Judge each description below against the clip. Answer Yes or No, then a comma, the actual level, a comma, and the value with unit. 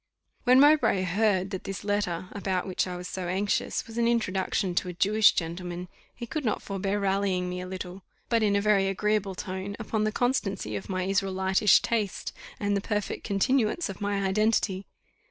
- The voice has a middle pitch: No, high, 195 Hz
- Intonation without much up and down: Yes, narrow, 2.3 semitones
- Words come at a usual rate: Yes, average, 185 wpm